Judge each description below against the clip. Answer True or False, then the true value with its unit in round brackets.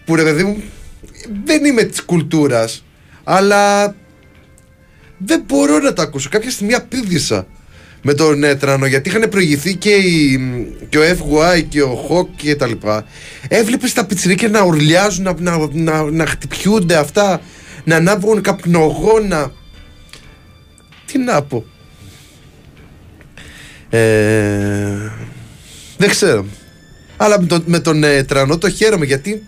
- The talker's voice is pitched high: False (155 Hz)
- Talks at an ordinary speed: True (125 wpm)